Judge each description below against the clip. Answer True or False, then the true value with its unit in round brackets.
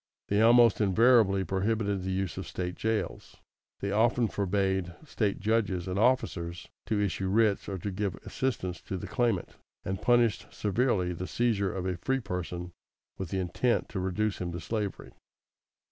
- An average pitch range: True (3.4 semitones)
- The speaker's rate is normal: True (160 wpm)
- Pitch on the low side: True (100 Hz)